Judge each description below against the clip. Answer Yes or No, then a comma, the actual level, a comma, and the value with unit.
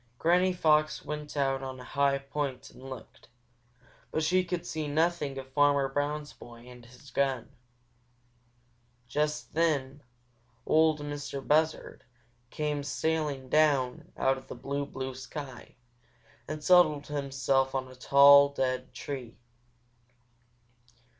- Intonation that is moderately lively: No, narrow, 2.3 semitones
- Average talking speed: No, slow, 125 wpm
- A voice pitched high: No, medium, 140 Hz